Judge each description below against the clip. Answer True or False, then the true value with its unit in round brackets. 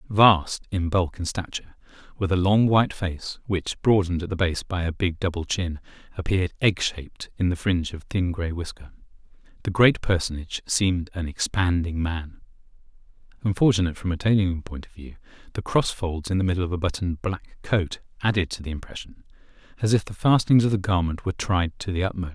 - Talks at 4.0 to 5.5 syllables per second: False (5.8 syllables/s)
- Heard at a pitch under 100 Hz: True (90 Hz)